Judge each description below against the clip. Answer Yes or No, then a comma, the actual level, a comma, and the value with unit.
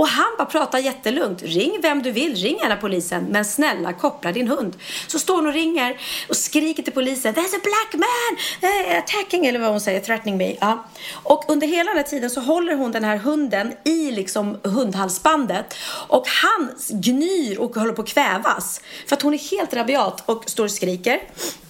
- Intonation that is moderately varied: No, wide, 6.0 semitones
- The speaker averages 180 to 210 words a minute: Yes, fast, 195 wpm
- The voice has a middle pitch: No, very high, 280 Hz